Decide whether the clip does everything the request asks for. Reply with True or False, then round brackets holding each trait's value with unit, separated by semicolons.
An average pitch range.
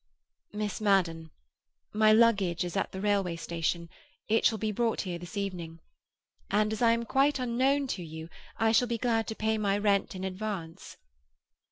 True (3.9 semitones)